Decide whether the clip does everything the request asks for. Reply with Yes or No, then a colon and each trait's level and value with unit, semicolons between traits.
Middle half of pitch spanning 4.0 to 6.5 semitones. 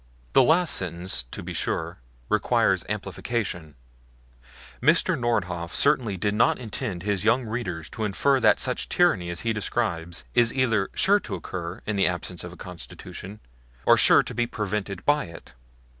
Yes: average, 5.2 semitones